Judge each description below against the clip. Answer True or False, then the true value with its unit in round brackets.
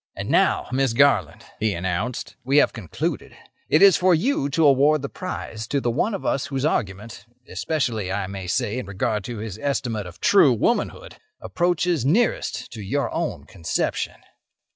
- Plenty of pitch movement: True (6.0 semitones)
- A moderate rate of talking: True (165 wpm)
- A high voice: False (125 Hz)